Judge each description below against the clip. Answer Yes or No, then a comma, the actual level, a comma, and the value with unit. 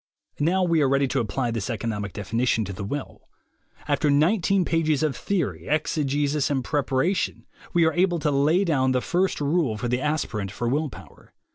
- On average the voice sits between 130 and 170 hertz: Yes, medium, 140 Hz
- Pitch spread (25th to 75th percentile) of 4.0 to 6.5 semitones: Yes, average, 5.1 semitones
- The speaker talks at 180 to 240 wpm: Yes, average, 185 wpm